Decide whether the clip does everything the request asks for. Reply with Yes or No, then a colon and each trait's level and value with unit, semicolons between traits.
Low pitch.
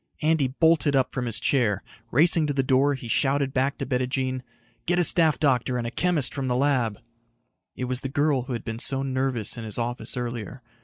Yes: low, 130 Hz